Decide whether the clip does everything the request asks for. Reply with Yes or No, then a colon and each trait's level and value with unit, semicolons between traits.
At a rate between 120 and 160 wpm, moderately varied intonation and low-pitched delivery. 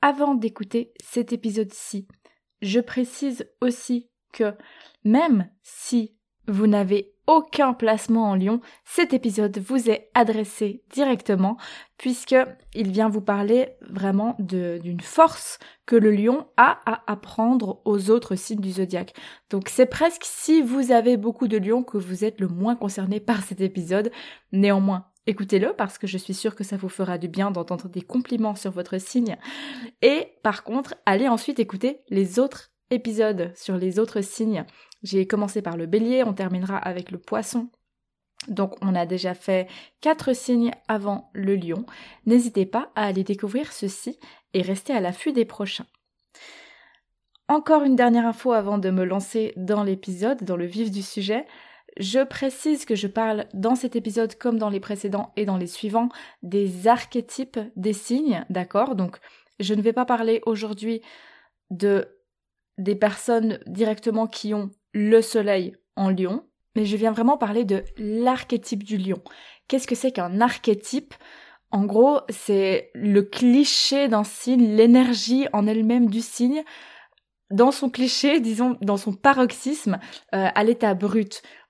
No: average, 155 wpm; average, 3.7 semitones; high, 220 Hz